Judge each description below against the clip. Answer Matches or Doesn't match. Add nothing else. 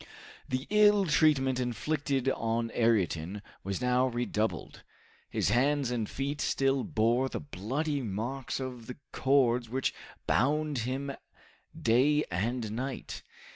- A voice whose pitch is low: Matches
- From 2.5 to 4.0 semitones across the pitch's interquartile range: Matches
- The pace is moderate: Doesn't match